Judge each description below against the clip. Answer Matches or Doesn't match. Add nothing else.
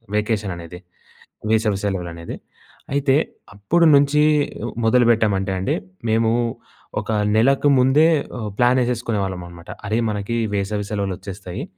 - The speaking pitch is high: Doesn't match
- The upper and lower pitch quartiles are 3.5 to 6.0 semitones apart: Matches